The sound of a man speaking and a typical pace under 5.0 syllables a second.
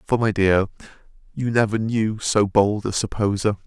Yes: male; 4.7 syllables/s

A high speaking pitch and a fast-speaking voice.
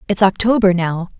No: high, 195 Hz; average, 150 wpm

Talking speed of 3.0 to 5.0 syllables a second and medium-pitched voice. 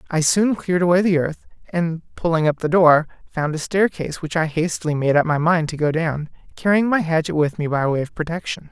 No: 5.6 syllables/s; medium, 165 Hz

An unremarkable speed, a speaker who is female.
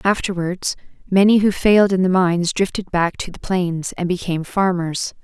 Yes: average, 170 wpm; female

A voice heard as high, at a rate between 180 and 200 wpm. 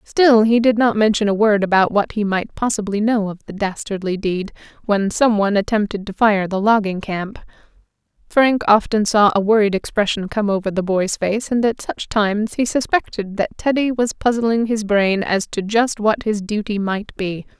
Yes: high, 210 Hz; average, 195 wpm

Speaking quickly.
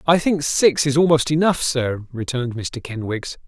No: average, 175 wpm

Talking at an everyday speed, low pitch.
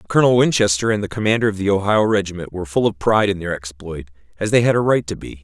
No: fast, 265 wpm; low, 100 Hz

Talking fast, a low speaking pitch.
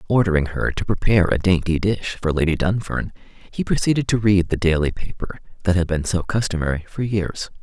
No: average, 190 wpm; very low, 90 Hz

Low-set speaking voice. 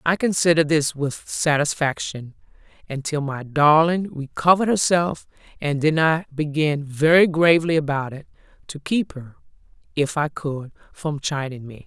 No: medium, 150 Hz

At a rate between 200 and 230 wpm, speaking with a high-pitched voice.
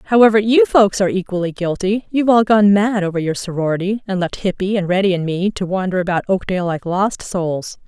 Yes: fast, 205 wpm; high, 195 Hz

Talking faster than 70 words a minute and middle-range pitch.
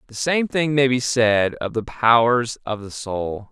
No: fast, 205 wpm; low, 120 Hz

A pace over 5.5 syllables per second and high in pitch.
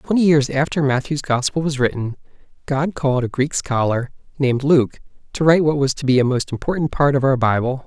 No: 5.8 syllables/s; medium, 140 Hz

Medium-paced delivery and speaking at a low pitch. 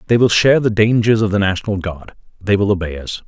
No: fast, 240 wpm; low, 100 Hz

